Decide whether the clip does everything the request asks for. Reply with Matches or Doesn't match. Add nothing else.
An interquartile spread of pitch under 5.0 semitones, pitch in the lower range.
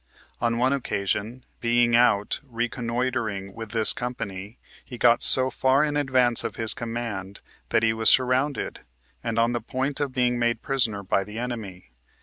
Matches